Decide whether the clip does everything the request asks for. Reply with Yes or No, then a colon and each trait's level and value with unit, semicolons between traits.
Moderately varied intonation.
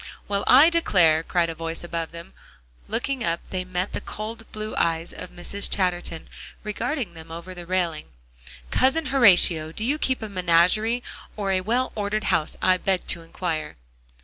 Yes: average, 4.6 semitones